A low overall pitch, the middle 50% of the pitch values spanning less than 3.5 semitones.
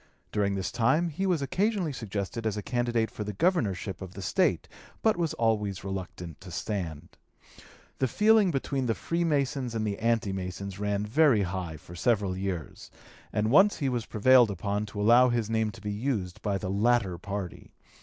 No: low, 110 Hz; average, 4.8 semitones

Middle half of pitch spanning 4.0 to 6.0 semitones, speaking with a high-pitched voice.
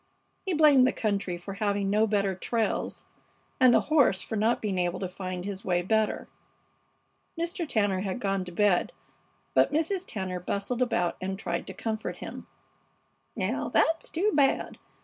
Yes: average, 4.9 semitones; high, 205 Hz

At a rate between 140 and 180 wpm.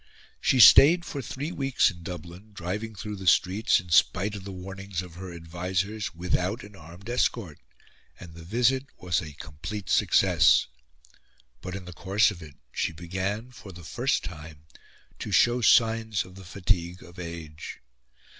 Yes: average, 165 wpm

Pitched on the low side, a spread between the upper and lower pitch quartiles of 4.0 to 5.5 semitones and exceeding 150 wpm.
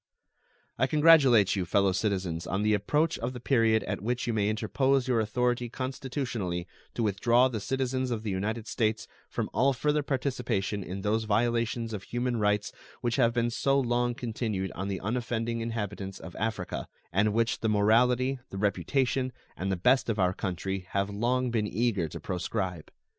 No: low, 115 Hz; average, 3.6 semitones; average, 175 wpm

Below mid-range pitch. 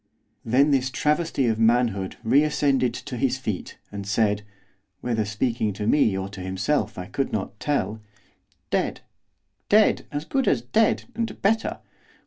Yes: low, 120 Hz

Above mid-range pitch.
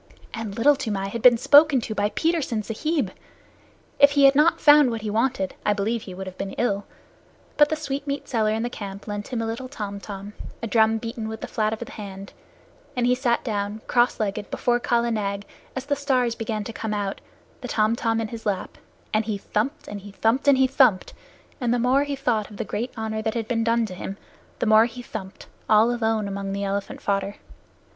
Yes: high, 225 Hz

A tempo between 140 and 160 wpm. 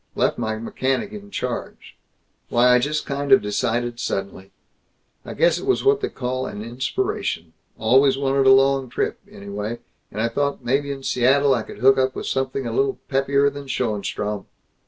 No: average, 175 wpm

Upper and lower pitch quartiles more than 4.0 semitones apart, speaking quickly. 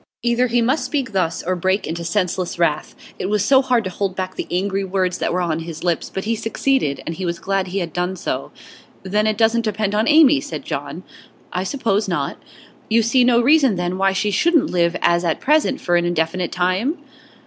Yes: average, 4.7 semitones; fast, 215 wpm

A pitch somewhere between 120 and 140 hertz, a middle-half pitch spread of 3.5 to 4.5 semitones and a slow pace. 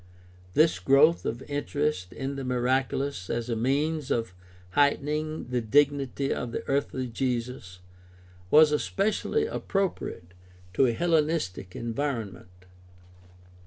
Yes: low, 135 Hz; average, 4.2 semitones; slow, 110 wpm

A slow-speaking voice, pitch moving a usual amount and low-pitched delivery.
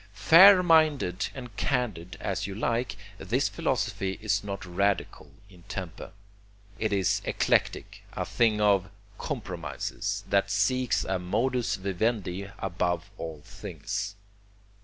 Yes: slow, 115 wpm; average, 4.4 semitones; low, 100 Hz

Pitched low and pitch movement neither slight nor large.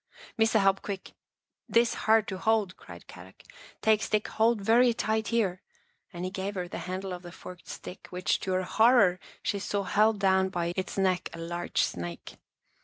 No: high, 195 Hz; average, 3.2 semitones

